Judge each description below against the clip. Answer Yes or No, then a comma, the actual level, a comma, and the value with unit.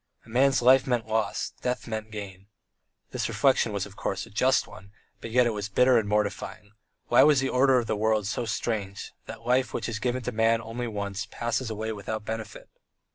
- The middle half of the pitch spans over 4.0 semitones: No, average, 2.9 semitones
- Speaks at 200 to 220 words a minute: Yes, fast, 205 wpm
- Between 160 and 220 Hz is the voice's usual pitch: No, low, 110 Hz